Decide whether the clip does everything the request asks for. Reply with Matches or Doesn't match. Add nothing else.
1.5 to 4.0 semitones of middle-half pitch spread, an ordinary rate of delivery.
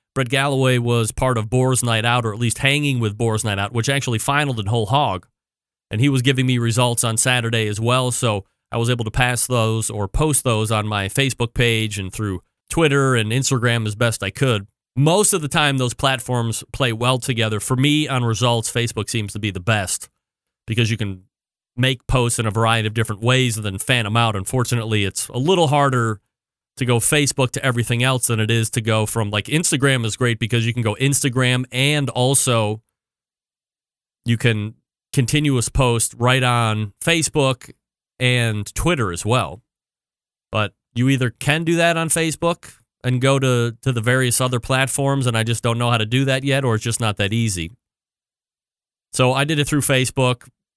Matches